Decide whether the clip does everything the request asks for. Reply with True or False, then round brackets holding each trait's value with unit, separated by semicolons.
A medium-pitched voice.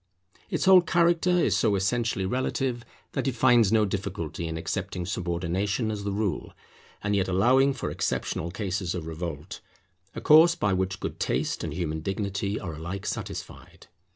False (100 Hz)